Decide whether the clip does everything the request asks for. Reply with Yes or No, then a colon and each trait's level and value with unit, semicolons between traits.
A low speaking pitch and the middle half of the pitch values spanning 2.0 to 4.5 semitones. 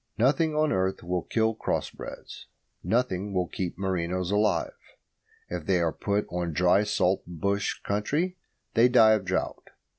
Yes: low, 100 Hz; average, 3.7 semitones